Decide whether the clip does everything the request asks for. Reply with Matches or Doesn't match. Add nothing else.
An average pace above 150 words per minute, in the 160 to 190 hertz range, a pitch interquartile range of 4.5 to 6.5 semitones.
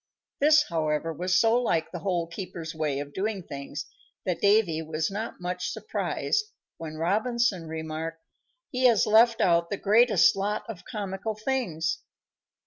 Doesn't match